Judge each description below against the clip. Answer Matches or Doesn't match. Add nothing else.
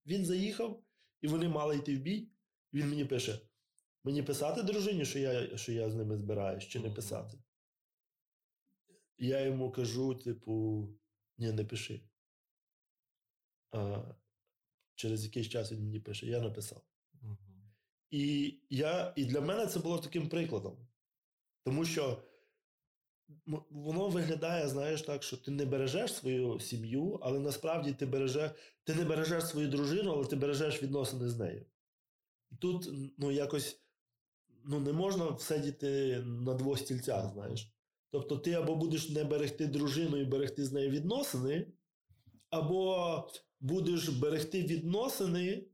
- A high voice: Doesn't match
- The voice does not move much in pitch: Doesn't match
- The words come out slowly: Doesn't match